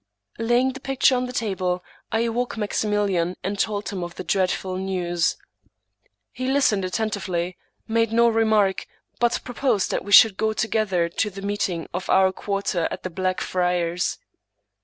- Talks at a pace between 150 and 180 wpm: Yes, average, 160 wpm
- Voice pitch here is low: No, high, 200 Hz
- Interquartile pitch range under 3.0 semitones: No, average, 3.6 semitones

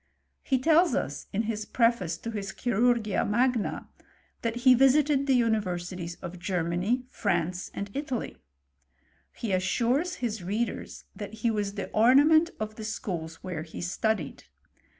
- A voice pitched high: Yes, high, 220 Hz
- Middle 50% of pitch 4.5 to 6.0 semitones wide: Yes, average, 5.0 semitones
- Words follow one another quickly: No, average, 150 wpm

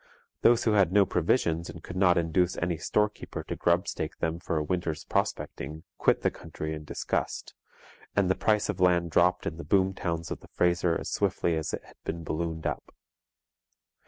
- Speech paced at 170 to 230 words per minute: Yes, average, 190 wpm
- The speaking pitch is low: Yes, very low, 85 Hz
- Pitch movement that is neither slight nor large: No, narrow, 2.3 semitones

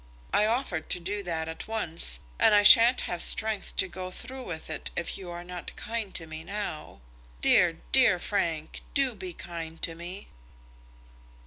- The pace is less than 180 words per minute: Yes, average, 170 wpm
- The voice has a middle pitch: Yes, medium, 180 Hz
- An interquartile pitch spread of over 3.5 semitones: Yes, average, 4.2 semitones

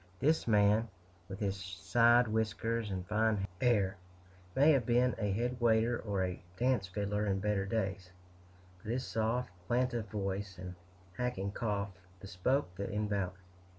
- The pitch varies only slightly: No, average, 3.4 semitones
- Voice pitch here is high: No, low, 105 Hz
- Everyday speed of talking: Yes, average, 145 wpm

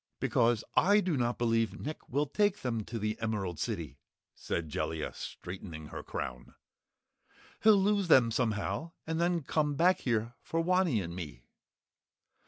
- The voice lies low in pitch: Yes, low, 120 Hz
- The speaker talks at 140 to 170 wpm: Yes, average, 150 wpm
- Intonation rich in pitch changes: Yes, wide, 8.4 semitones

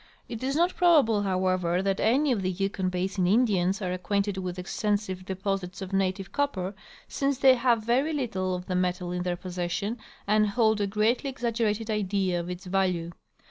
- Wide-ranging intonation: No, average, 3.7 semitones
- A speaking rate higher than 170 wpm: Yes, average, 180 wpm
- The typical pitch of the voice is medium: No, high, 195 Hz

